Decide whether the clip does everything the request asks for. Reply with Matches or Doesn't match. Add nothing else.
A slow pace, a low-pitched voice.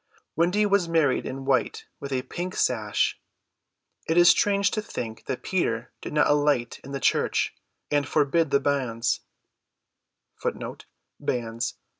Doesn't match